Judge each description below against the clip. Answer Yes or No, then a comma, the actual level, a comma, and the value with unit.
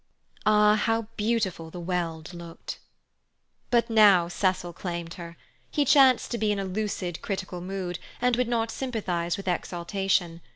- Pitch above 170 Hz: Yes, high, 190 Hz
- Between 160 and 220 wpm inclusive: No, average, 150 wpm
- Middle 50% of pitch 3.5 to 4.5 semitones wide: Yes, average, 4.2 semitones